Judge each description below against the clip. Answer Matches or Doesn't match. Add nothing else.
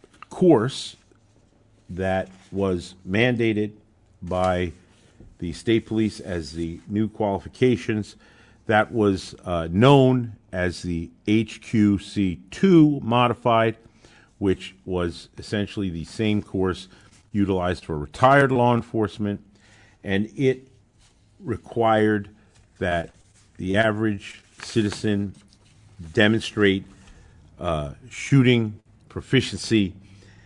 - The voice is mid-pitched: Doesn't match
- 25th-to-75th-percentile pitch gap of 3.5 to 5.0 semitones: Doesn't match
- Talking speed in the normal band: Doesn't match